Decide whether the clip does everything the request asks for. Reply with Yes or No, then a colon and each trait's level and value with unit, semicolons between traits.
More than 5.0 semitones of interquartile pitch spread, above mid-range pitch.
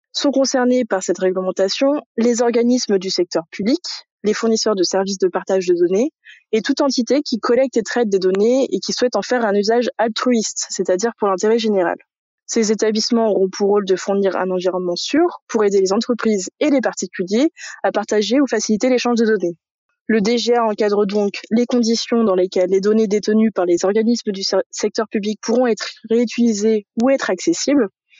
No: average, 3.8 semitones; high, 220 Hz